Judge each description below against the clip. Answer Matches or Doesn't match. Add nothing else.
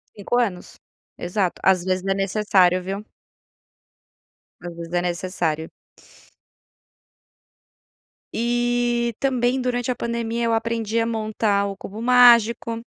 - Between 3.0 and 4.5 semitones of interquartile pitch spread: Matches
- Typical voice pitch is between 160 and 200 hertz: Doesn't match